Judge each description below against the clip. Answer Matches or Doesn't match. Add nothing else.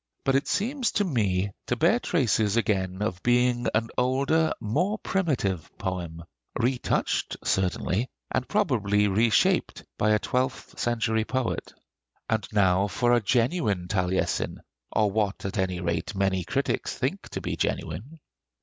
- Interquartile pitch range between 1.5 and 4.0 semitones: Doesn't match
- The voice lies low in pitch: Matches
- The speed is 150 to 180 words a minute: Doesn't match